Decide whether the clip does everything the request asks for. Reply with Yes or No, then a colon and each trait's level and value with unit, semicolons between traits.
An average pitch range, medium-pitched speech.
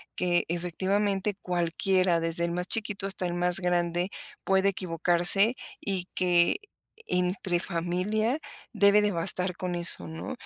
No: narrow, 2.1 semitones; medium, 180 Hz